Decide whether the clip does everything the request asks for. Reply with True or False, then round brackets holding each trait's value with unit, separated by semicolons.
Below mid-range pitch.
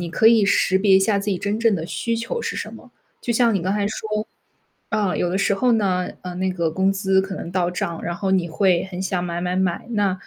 False (190 Hz)